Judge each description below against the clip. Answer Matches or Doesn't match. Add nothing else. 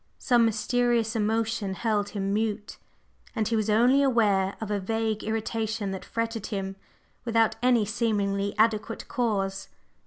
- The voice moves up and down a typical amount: Doesn't match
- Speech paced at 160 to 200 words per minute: Doesn't match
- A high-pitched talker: Matches